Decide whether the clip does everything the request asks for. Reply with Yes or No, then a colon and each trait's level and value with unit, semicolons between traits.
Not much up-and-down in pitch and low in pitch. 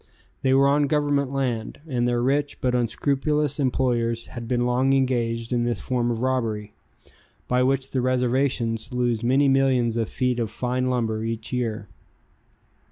Yes: narrow, 2.3 semitones; low, 125 Hz